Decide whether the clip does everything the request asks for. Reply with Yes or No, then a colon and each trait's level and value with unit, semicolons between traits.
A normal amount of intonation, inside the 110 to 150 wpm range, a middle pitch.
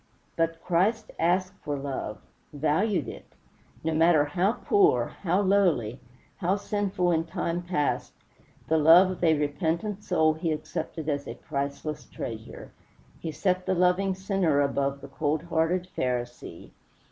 Yes: average, 4.0 semitones; average, 140 wpm; medium, 165 Hz